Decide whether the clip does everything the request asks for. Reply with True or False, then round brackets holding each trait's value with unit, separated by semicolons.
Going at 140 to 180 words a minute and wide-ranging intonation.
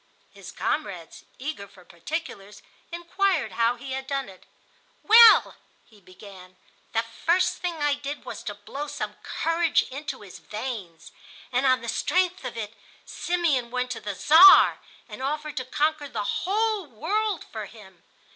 True (155 wpm; 7.5 semitones)